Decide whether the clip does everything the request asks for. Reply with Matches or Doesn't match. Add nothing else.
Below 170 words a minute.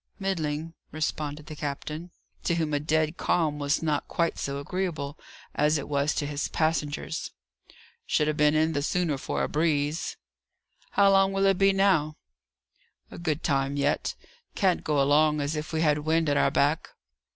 Doesn't match